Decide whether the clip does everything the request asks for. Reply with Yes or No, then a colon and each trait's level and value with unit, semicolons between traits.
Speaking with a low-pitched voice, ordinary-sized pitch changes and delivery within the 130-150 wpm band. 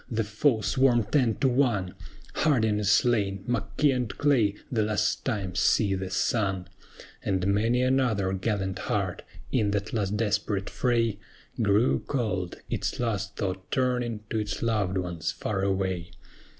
Yes: low, 105 Hz; average, 3.6 semitones; average, 145 wpm